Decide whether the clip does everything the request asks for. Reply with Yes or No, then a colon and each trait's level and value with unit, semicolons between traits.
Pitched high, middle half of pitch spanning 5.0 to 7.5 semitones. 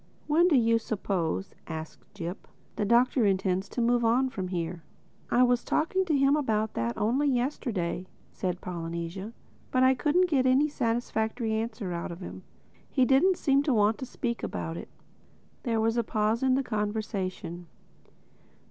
Yes: high, 225 Hz; wide, 5.5 semitones